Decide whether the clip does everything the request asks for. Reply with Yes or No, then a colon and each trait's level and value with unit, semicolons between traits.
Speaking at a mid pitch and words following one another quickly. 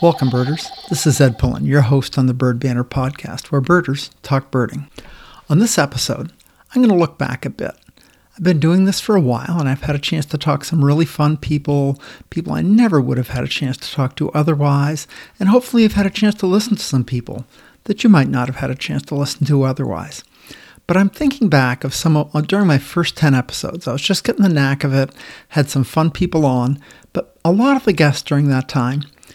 Yes: medium, 145 Hz; fast, 230 wpm